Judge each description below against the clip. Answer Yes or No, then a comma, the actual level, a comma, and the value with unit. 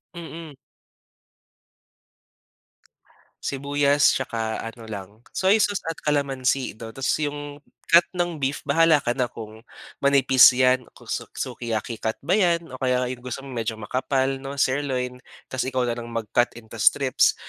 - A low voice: Yes, low, 130 Hz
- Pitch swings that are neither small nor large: Yes, average, 3.2 semitones